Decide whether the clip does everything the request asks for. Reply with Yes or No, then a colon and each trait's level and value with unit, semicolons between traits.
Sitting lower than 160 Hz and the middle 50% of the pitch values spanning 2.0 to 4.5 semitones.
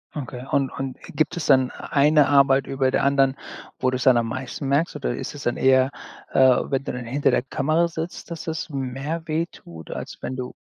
Yes: low, 135 Hz; narrow, 2.4 semitones